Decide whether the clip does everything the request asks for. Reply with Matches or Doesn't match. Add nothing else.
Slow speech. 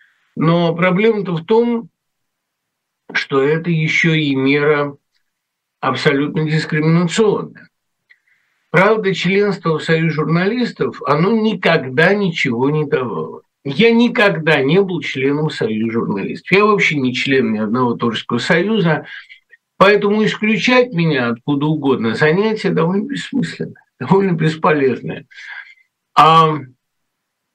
Matches